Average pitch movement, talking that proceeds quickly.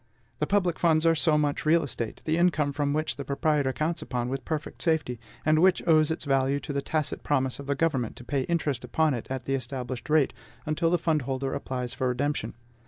Yes: average, 3.1 semitones; fast, 220 wpm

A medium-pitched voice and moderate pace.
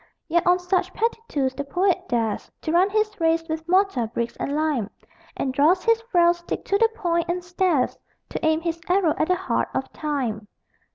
No: very high, 340 Hz; average, 195 wpm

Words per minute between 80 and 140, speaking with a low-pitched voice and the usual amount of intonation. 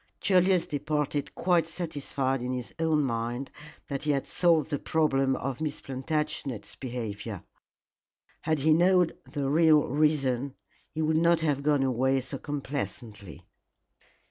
No: slow, 135 wpm; medium, 145 Hz; average, 3.3 semitones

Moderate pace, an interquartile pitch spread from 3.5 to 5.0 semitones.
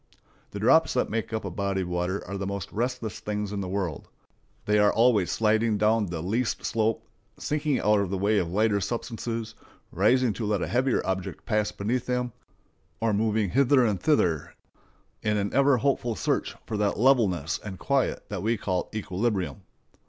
No: average, 180 wpm; average, 3.0 semitones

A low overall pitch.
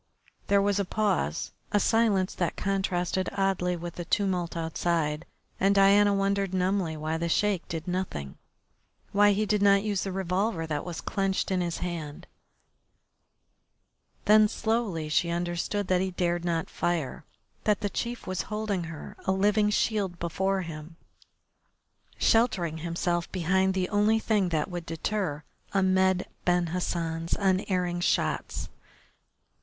No: medium, 185 Hz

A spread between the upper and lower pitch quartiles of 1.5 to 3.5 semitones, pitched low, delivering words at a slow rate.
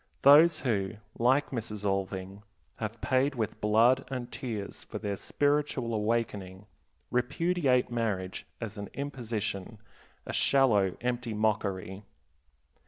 No: average, 4.1 semitones; low, 115 Hz; slow, 110 wpm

